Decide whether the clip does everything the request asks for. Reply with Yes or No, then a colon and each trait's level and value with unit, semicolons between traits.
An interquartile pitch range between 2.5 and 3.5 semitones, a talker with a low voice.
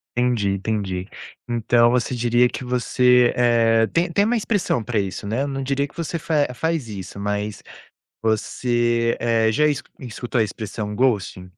Yes: average, 2.9 semitones; low, 120 Hz